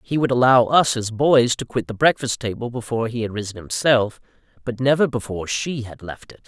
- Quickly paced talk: Yes, fast, 215 wpm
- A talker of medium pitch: No, low, 120 Hz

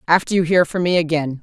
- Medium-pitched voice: Yes, medium, 165 Hz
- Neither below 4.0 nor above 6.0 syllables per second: No, 6.3 syllables/s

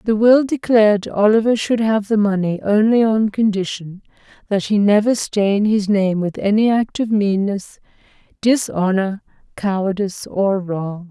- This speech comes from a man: No, female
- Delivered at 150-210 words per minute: No, average, 140 wpm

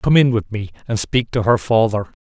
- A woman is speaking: No, male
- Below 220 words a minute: No, fast, 240 wpm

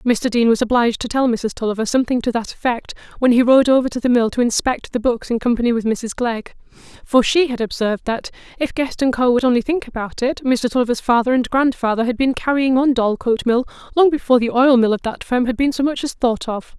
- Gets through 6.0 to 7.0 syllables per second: Yes, 6.1 syllables/s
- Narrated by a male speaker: No, female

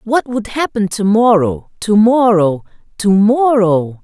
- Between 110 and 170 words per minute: Yes, slow, 135 wpm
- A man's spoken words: No, female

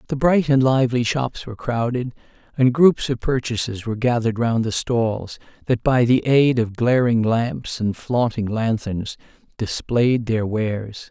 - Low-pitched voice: Yes, low, 115 Hz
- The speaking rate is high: No, average, 155 wpm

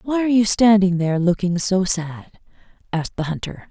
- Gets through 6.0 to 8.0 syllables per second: No, 5.6 syllables/s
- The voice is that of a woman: Yes, female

